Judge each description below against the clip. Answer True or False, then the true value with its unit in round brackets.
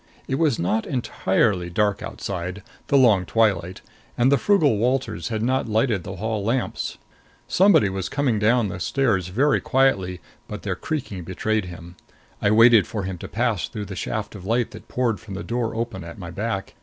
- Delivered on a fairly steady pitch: False (4.3 semitones)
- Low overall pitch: True (110 Hz)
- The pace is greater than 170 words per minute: True (185 wpm)